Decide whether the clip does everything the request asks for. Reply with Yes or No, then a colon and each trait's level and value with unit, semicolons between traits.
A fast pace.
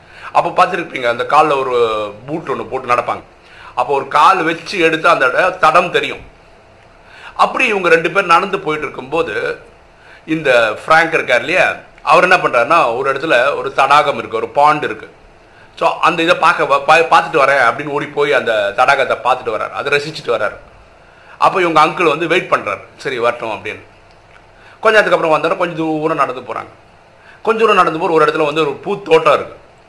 Yes: fast, 160 wpm